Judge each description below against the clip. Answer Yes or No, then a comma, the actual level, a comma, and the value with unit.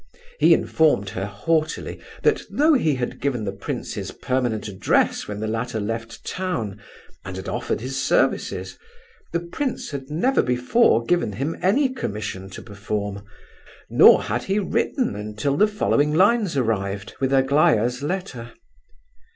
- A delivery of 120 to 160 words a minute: Yes, average, 145 wpm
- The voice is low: Yes, low, 125 Hz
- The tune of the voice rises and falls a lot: Yes, wide, 7.8 semitones